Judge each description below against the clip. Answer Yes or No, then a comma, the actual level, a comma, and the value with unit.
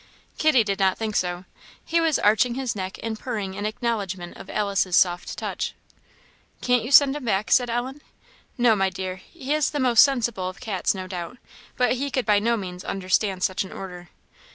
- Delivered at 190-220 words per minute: Yes, average, 195 wpm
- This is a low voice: No, high, 215 Hz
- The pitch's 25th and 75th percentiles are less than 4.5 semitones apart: No, average, 4.8 semitones